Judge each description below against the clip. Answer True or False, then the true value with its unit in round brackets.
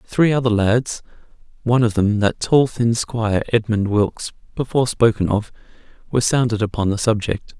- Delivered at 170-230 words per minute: False (140 wpm)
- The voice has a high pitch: False (115 Hz)